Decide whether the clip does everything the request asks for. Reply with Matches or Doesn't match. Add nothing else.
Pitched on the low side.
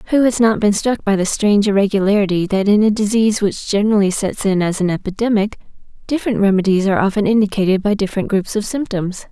Doesn't match